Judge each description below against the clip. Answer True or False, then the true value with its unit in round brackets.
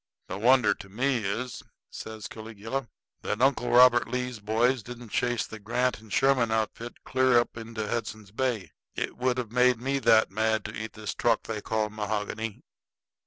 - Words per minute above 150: True (170 wpm)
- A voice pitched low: True (115 Hz)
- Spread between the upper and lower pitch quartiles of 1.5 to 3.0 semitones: True (2.5 semitones)